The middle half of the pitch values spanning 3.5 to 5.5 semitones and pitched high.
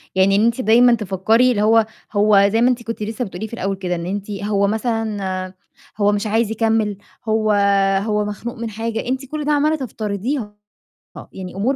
No: narrow, 2.6 semitones; high, 215 Hz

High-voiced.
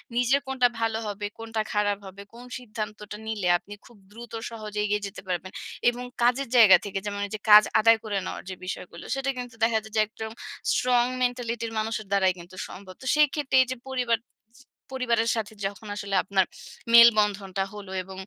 Yes: high, 220 Hz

